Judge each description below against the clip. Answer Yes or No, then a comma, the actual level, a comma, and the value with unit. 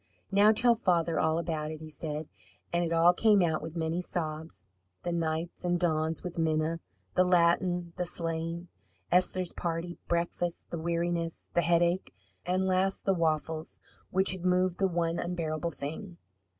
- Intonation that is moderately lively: No, narrow, 1.8 semitones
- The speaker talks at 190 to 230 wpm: No, average, 160 wpm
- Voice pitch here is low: No, medium, 170 Hz